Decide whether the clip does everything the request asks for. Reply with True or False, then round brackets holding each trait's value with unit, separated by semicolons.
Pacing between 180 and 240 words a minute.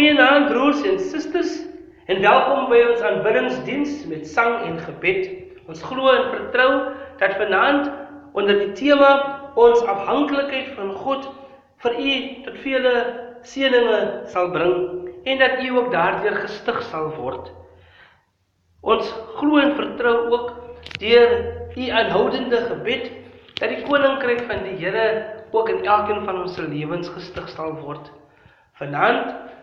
False (140 wpm)